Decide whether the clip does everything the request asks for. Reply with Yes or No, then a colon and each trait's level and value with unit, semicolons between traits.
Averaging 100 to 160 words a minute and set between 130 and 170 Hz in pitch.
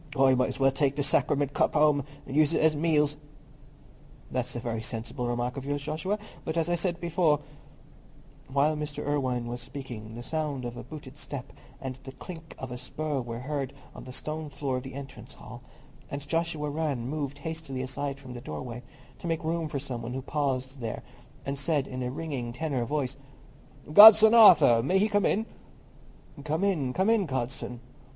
No: average, 190 wpm; medium, 140 Hz